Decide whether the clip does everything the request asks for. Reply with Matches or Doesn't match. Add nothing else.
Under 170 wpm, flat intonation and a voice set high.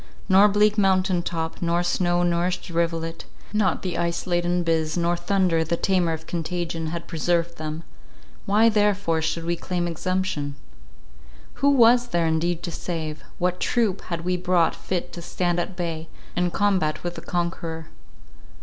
Doesn't match